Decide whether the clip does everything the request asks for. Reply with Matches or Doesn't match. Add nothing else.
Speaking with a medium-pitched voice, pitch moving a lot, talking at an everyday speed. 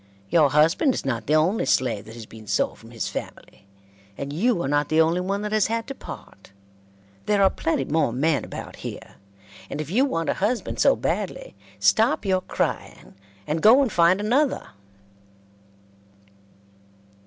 Matches